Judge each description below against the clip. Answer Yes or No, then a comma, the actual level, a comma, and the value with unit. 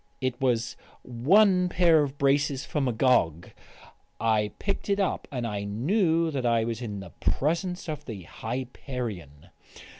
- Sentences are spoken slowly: No, average, 145 wpm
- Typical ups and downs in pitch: No, wide, 6.0 semitones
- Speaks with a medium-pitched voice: No, low, 130 Hz